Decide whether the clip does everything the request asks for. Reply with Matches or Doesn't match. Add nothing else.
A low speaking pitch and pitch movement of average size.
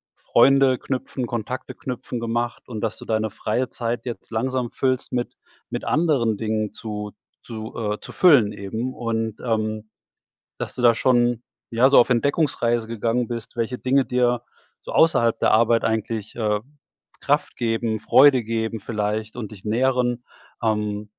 Doesn't match